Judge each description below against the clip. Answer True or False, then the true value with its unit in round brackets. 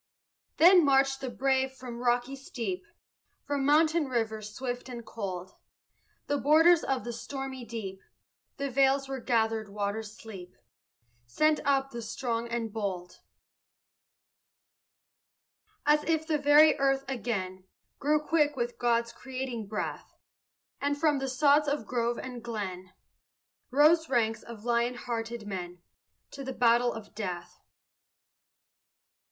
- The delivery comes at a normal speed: False (125 wpm)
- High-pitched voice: True (245 Hz)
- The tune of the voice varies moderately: True (3.8 semitones)